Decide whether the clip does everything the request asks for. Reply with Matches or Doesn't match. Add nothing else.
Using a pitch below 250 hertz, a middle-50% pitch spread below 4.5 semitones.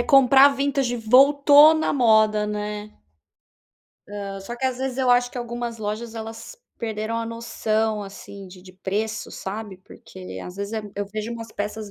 Matches